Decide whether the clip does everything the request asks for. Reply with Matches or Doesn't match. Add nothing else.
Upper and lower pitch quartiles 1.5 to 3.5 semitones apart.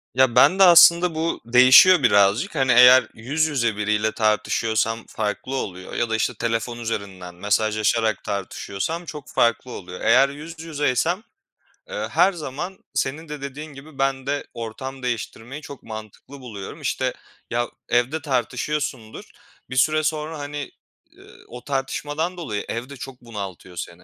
Doesn't match